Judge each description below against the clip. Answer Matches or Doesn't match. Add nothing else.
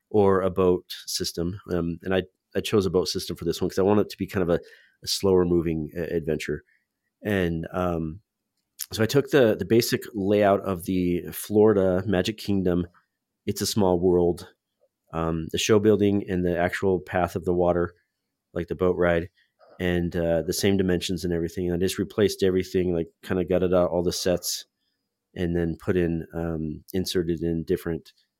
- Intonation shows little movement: Matches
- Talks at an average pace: Matches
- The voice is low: Matches